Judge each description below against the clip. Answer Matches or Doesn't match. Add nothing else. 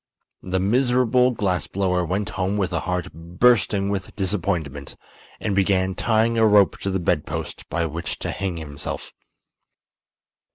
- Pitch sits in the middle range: Doesn't match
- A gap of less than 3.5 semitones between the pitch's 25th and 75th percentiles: Matches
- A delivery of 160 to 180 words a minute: Doesn't match